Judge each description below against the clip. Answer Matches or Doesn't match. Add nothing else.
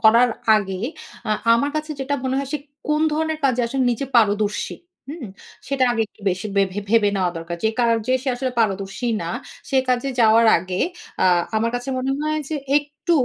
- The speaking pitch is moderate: Doesn't match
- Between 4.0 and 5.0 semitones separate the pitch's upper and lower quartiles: Matches